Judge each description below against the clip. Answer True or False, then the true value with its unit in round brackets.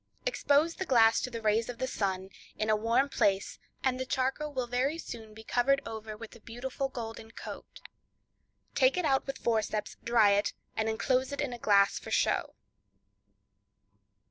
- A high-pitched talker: True (235 Hz)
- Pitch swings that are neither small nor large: True (3.3 semitones)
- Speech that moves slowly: False (175 wpm)